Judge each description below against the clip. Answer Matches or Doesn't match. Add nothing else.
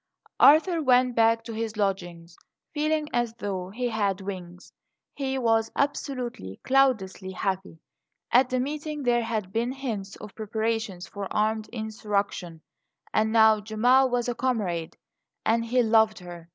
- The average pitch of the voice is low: Doesn't match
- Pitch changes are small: Doesn't match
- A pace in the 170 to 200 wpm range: Doesn't match